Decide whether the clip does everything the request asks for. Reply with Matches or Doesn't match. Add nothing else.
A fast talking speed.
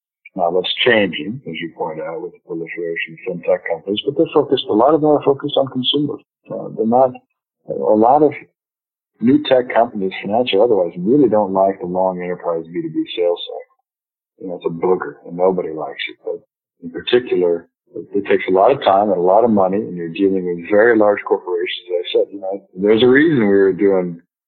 Matches